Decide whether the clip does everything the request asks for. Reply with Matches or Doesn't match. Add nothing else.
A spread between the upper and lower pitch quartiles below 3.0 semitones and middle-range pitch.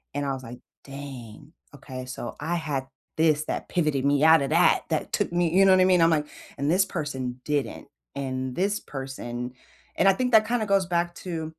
Doesn't match